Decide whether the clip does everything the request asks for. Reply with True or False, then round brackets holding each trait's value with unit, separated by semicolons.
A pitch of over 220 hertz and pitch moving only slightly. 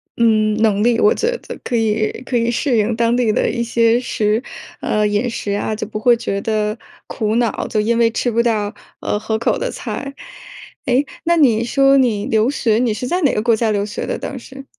True (230 Hz; 2.3 semitones)